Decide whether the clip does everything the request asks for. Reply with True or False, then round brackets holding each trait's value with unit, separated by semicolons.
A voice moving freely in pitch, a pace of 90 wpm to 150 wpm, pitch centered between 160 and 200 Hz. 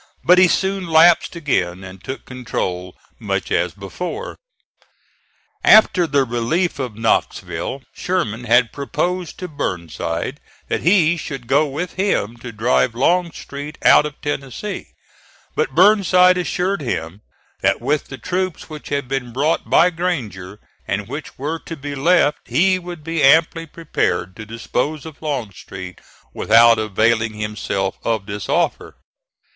False (7.2 semitones; 140 wpm; 140 Hz)